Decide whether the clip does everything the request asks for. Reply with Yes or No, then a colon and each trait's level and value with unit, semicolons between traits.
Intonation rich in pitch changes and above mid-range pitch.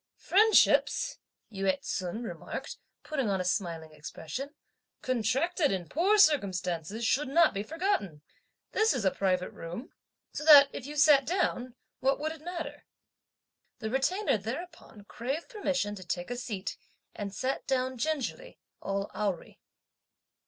Yes: wide, 7.8 semitones; very high, 255 Hz